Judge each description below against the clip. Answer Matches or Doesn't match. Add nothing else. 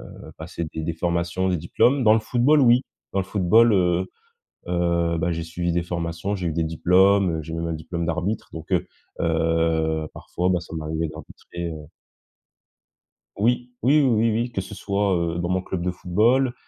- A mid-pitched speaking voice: Doesn't match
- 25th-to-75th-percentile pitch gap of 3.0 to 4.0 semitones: Matches